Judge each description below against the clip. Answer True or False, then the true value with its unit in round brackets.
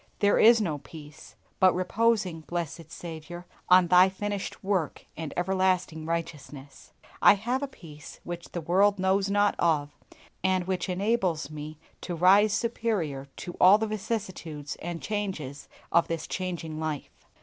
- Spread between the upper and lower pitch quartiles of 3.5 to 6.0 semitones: True (3.9 semitones)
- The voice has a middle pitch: True (180 Hz)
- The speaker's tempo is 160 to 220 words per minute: False (145 wpm)